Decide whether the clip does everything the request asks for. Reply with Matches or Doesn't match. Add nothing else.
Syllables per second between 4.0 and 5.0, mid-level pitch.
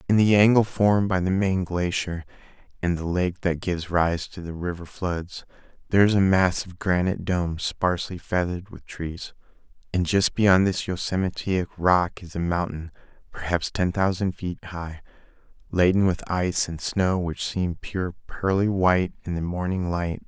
Doesn't match